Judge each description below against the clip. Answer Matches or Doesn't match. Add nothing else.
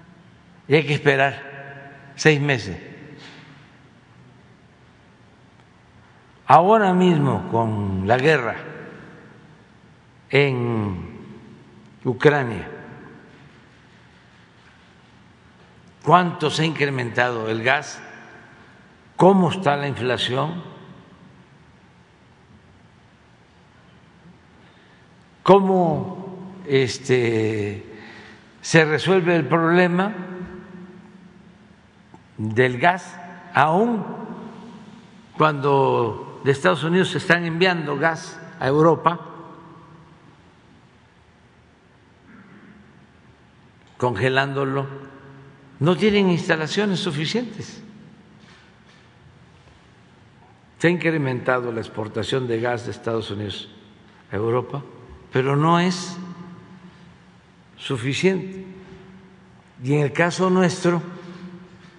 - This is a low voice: Doesn't match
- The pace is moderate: Doesn't match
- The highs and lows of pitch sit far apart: Doesn't match